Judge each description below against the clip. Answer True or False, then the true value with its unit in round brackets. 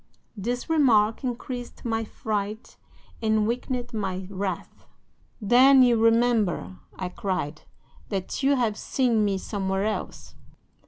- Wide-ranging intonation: False (3.7 semitones)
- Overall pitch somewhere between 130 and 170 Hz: False (220 Hz)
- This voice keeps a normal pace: False (115 wpm)